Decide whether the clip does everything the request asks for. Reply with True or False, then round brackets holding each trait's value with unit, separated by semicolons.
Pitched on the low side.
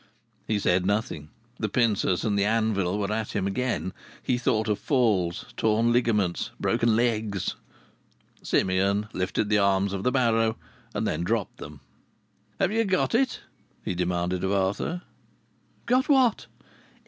True (105 Hz)